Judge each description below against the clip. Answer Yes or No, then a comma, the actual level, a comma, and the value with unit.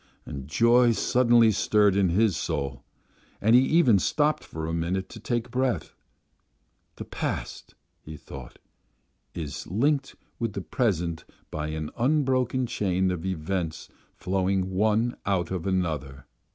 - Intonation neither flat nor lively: No, wide, 6.4 semitones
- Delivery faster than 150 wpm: No, slow, 135 wpm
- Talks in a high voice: No, very low, 95 Hz